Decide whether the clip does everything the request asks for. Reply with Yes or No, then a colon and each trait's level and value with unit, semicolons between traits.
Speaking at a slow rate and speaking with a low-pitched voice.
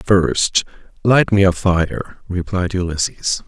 Yes: slow, 120 wpm; very low, 95 Hz